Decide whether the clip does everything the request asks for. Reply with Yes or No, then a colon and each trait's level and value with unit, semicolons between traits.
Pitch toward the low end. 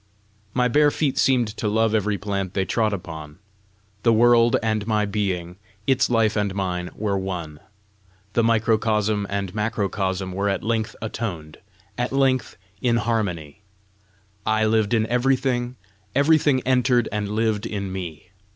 Yes: low, 110 Hz